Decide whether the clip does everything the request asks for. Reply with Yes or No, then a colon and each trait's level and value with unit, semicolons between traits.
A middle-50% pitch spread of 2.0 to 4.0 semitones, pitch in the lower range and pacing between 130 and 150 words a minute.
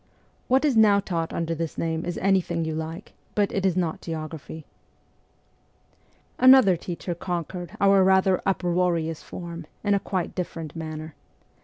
No: average, 2.9 semitones; medium, 175 Hz; average, 145 wpm